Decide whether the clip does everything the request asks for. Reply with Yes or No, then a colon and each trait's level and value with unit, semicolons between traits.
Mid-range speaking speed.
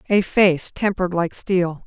Yes: average, 160 wpm